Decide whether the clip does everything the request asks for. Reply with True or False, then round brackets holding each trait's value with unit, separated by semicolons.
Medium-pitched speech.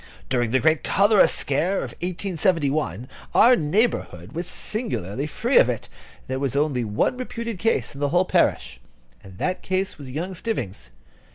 True (155 Hz)